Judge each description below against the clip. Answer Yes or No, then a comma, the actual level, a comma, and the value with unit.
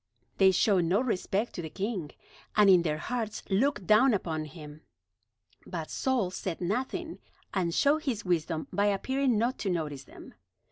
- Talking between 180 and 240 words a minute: No, average, 160 wpm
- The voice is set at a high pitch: Yes, high, 195 Hz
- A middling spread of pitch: No, wide, 5.9 semitones